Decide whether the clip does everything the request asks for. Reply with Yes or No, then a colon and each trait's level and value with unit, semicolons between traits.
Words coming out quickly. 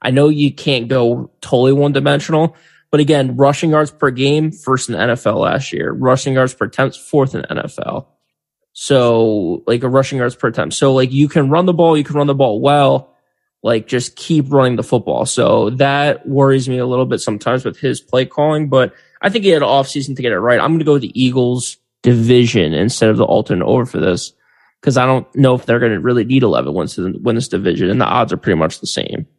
Yes: fast, 235 wpm